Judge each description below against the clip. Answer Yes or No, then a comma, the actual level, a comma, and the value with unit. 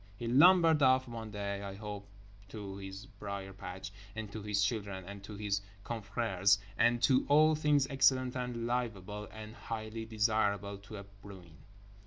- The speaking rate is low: No, average, 155 wpm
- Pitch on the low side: Yes, low, 105 Hz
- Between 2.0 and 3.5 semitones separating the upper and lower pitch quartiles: Yes, average, 3.2 semitones